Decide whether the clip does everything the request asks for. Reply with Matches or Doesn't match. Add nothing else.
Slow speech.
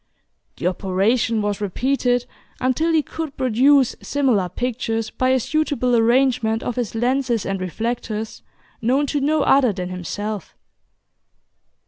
Matches